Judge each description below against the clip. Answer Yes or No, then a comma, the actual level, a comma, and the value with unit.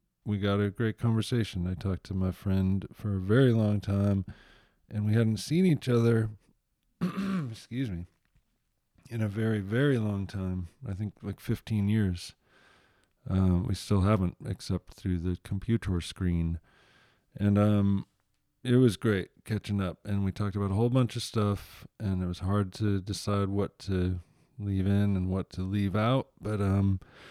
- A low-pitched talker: Yes, low, 100 Hz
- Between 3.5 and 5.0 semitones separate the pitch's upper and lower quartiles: No, average, 2.8 semitones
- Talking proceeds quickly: No, average, 165 wpm